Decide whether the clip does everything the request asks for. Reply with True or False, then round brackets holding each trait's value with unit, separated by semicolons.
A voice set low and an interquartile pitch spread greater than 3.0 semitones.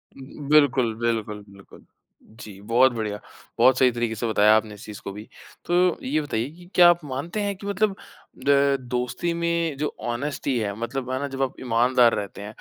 True (130 Hz; 5.0 semitones)